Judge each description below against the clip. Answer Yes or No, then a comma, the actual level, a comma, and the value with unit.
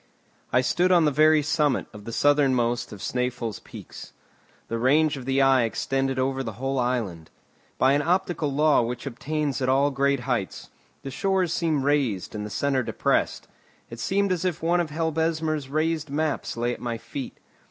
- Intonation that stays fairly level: No, average, 3.8 semitones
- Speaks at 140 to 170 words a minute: No, average, 180 wpm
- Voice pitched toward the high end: No, medium, 140 Hz